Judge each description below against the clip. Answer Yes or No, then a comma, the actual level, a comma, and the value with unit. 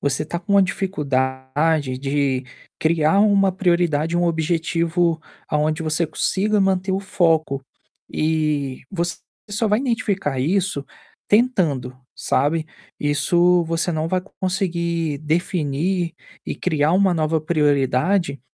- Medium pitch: Yes, medium, 165 Hz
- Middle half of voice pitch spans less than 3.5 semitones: No, average, 4.0 semitones